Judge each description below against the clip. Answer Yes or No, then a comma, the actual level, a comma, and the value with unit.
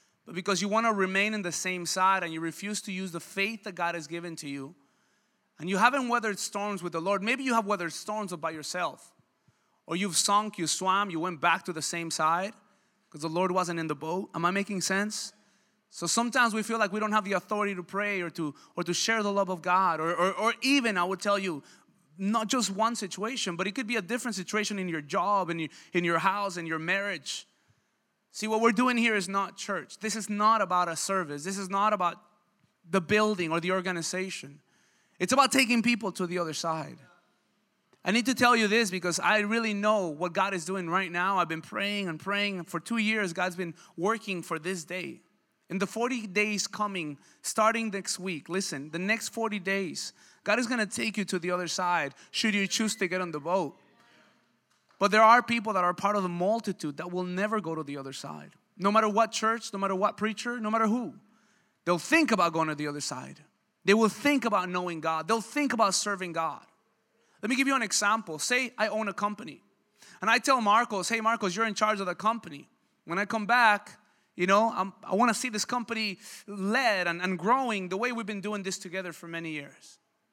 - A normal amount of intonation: Yes, average, 3.7 semitones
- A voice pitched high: Yes, high, 195 Hz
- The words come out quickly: Yes, fast, 225 wpm